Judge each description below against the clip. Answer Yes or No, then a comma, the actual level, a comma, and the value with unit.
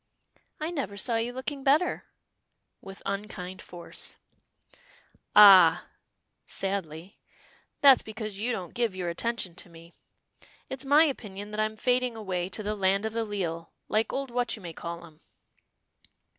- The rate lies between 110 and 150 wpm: Yes, average, 145 wpm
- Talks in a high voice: Yes, high, 210 Hz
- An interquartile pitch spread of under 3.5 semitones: No, average, 4.7 semitones